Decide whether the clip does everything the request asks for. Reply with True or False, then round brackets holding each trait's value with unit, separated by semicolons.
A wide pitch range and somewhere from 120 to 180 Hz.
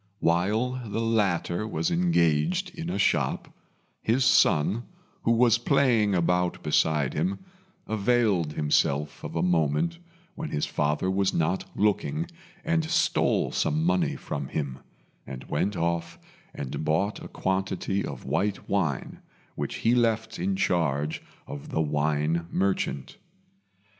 False (6.6 semitones; 95 Hz)